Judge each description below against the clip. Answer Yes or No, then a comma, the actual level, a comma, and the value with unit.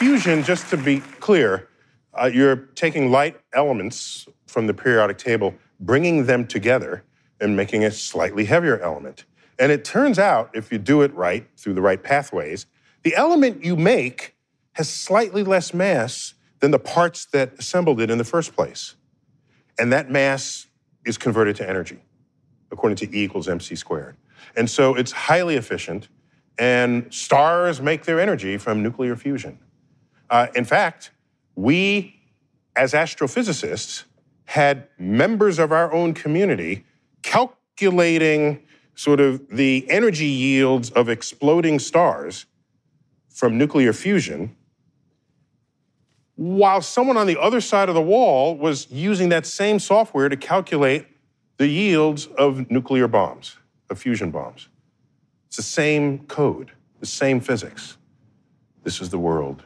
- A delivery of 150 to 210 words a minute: No, average, 140 wpm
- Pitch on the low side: No, medium, 145 Hz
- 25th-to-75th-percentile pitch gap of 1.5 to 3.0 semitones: No, average, 4.9 semitones